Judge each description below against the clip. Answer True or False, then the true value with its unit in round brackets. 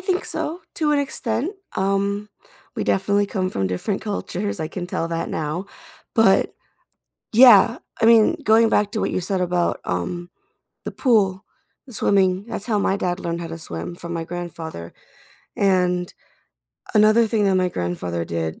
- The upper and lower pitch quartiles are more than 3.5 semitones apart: True (3.9 semitones)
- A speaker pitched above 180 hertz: True (190 Hz)